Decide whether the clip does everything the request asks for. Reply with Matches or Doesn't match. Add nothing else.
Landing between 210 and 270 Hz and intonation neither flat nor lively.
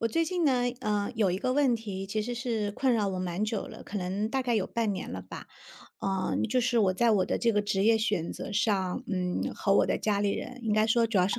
Matches